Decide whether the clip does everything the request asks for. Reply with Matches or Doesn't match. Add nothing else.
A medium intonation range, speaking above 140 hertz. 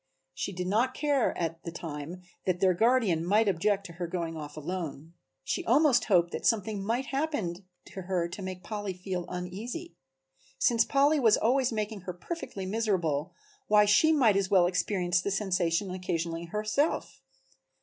Matches